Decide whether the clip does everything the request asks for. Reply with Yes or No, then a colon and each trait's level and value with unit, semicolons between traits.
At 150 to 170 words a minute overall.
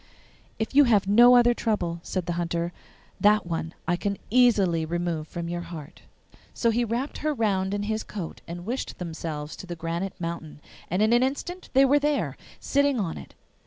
No: average, 190 wpm